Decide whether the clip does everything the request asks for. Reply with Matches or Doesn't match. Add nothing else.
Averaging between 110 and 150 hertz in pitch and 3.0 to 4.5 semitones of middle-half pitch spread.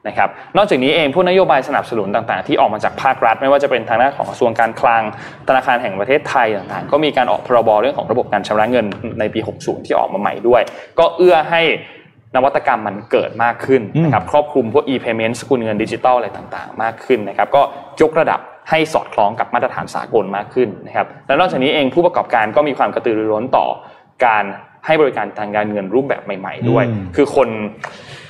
Doesn't match